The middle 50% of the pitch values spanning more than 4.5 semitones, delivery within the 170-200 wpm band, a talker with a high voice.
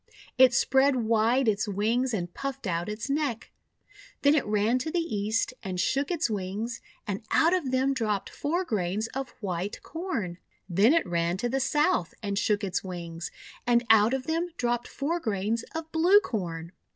Yes: wide, 5.5 semitones; average, 175 wpm; high, 230 Hz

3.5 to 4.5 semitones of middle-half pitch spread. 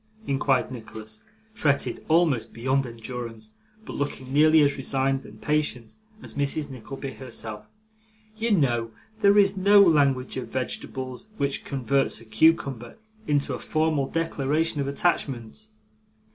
Yes: average, 3.8 semitones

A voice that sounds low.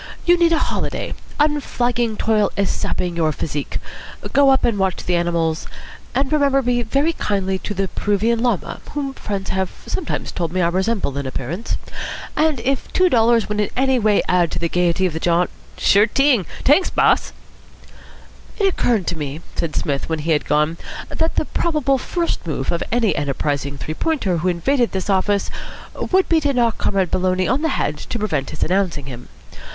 No: high, 200 Hz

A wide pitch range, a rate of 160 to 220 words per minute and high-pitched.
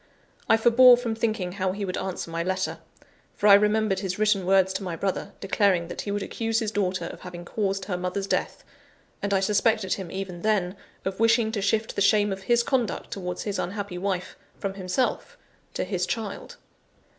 No: narrow, 2.6 semitones; average, 195 wpm; high, 195 Hz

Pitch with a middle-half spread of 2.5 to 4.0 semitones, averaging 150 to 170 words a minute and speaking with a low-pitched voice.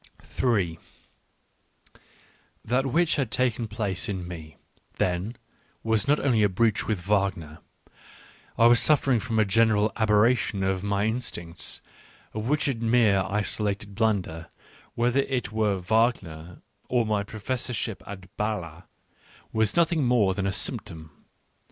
No: average, 3.7 semitones; slow, 135 wpm; low, 110 Hz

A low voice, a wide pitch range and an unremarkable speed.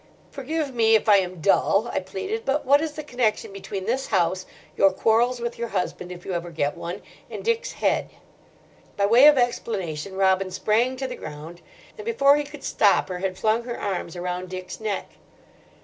No: high, 215 Hz; wide, 5.7 semitones; average, 195 wpm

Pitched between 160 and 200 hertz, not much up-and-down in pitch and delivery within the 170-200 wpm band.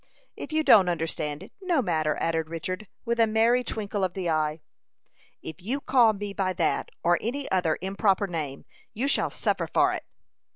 No: high, 190 Hz; wide, 5.6 semitones; average, 180 wpm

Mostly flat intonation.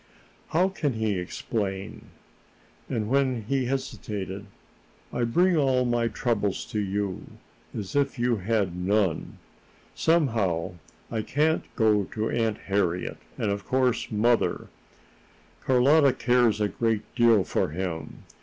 No: average, 4.1 semitones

